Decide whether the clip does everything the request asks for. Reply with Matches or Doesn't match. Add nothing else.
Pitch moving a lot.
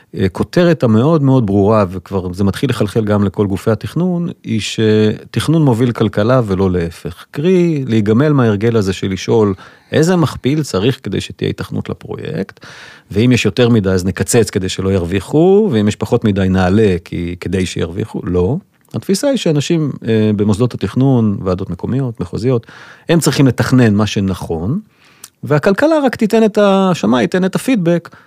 Matches